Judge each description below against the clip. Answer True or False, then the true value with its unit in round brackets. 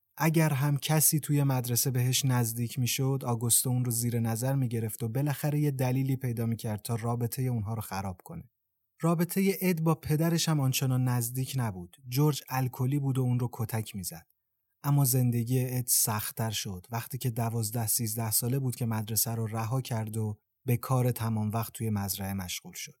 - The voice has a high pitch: False (125 Hz)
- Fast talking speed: True (175 wpm)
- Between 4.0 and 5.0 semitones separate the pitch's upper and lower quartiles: False (3.1 semitones)